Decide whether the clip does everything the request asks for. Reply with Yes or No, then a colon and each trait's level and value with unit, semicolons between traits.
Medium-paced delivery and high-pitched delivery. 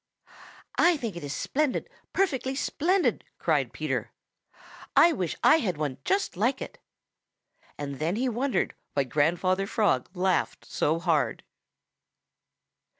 No: slow, 125 wpm; high, 195 Hz